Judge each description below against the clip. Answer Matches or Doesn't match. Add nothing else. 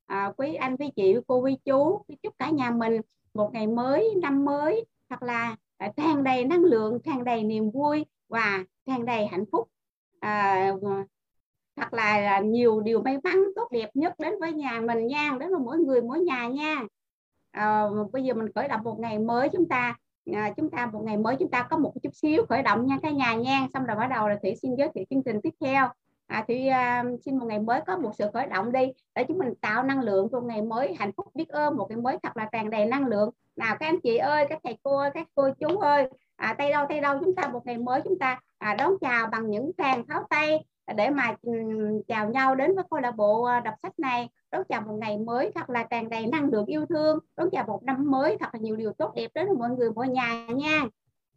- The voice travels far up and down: Doesn't match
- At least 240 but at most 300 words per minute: Matches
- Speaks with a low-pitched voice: Doesn't match